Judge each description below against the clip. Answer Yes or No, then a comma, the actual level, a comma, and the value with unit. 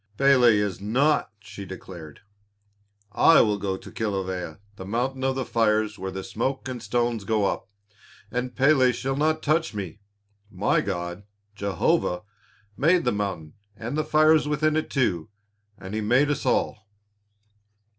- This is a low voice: Yes, low, 110 Hz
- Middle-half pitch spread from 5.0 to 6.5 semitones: Yes, wide, 5.5 semitones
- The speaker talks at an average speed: Yes, average, 150 wpm